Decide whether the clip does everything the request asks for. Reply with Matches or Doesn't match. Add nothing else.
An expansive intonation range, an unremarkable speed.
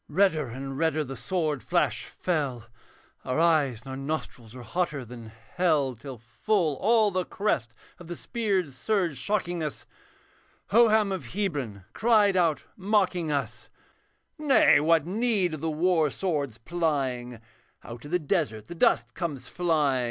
Matches